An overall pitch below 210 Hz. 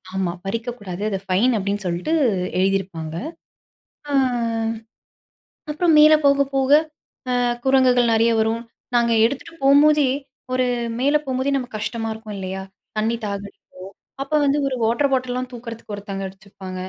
No: high, 230 Hz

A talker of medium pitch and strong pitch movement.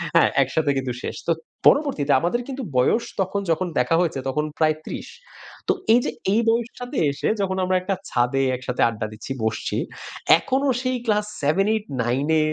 Yes: medium, 170 Hz; wide, 8.8 semitones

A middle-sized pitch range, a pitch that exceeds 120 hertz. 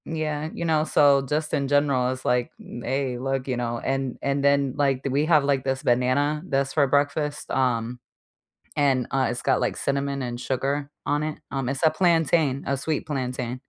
No: narrow, 2.2 semitones; medium, 140 Hz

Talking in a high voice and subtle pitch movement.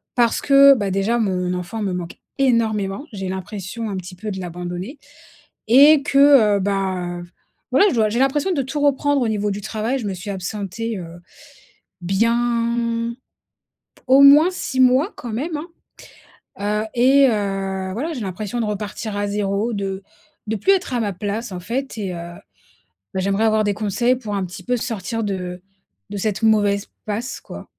No: high, 215 Hz; average, 4.1 semitones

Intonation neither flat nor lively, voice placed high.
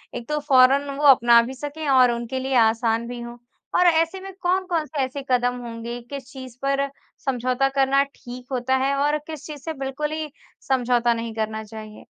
Yes: average, 3.2 semitones; very high, 265 Hz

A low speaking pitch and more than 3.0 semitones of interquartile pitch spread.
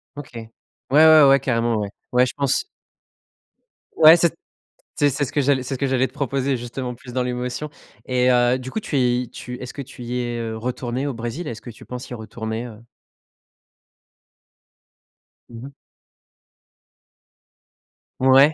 No: low, 125 Hz; narrow, 2.4 semitones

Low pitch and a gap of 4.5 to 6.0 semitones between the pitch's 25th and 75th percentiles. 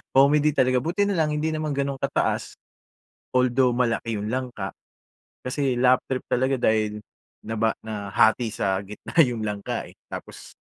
No: low, 125 Hz; average, 4.0 semitones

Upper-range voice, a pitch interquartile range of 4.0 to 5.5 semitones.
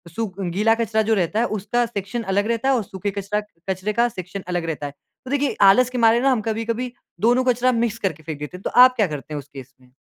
Yes: high, 215 Hz; average, 4.6 semitones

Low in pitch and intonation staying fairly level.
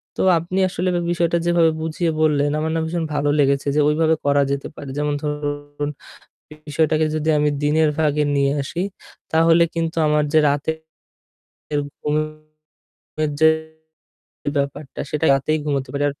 No: medium, 155 Hz; narrow, 1.7 semitones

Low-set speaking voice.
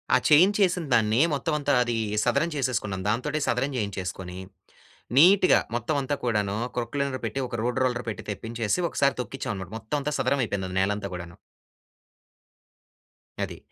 Yes: low, 120 Hz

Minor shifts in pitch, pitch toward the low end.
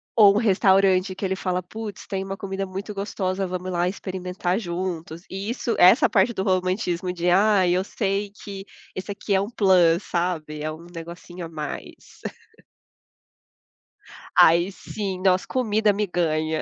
No: narrow, 2.1 semitones; medium, 185 Hz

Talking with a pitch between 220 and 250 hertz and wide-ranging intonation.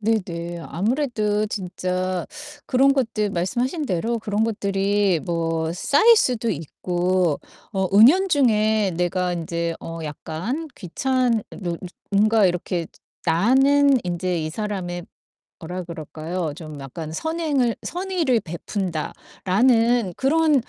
No: high, 200 Hz; wide, 6.0 semitones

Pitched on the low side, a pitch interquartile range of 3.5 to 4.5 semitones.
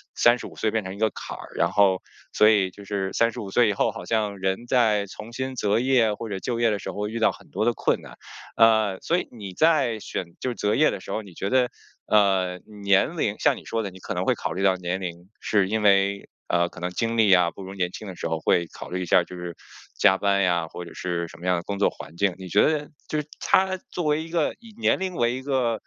Yes: low, 100 Hz; average, 3.9 semitones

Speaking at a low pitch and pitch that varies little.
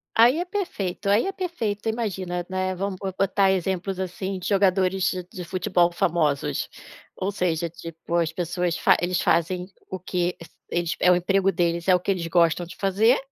No: medium, 185 Hz; narrow, 2.1 semitones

